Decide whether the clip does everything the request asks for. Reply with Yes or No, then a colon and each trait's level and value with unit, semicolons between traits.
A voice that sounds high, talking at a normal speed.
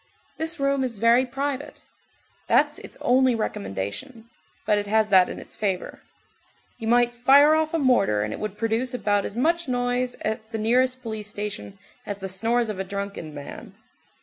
Yes: high, 225 Hz; average, 175 wpm